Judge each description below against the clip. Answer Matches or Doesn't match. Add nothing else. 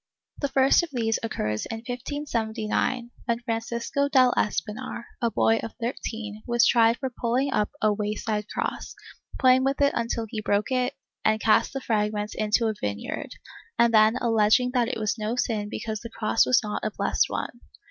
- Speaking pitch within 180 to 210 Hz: Doesn't match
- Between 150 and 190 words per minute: Matches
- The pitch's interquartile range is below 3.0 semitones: Matches